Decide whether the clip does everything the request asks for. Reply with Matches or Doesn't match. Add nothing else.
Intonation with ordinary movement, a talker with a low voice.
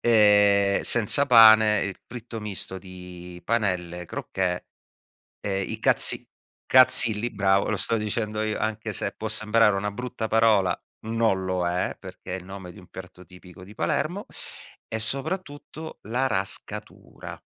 Matches